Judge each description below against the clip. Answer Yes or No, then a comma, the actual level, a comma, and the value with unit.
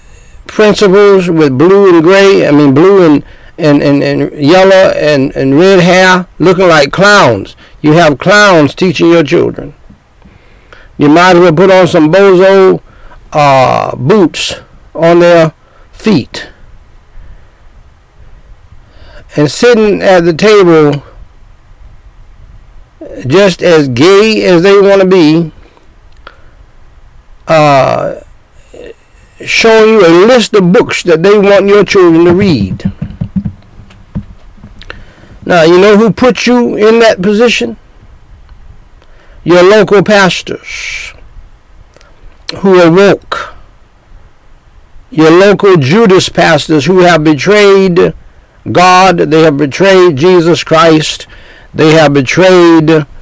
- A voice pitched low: No, medium, 180 Hz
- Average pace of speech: No, slow, 110 wpm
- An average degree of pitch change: Yes, average, 4.2 semitones